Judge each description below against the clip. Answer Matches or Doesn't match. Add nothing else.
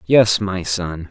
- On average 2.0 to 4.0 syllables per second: Matches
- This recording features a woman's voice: Doesn't match